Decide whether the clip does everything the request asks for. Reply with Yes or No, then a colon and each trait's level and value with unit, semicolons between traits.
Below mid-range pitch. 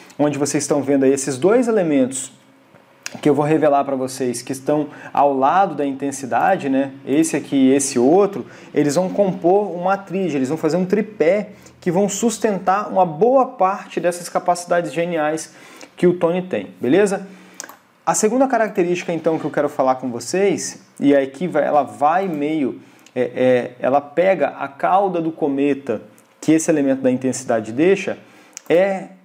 No: medium, 160 Hz